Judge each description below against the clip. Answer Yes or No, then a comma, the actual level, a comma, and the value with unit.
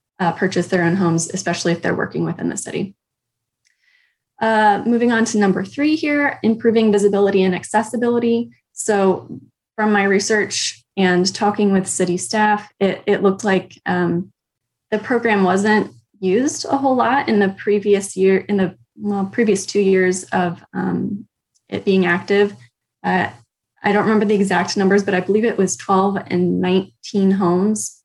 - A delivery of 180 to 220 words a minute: No, average, 160 wpm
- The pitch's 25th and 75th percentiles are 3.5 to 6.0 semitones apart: No, narrow, 2.5 semitones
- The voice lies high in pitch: Yes, high, 200 Hz